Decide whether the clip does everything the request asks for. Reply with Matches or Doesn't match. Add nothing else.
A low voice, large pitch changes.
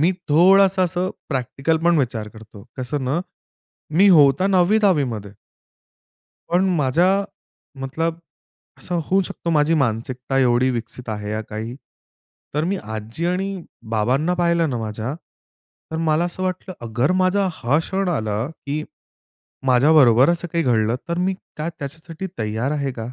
Doesn't match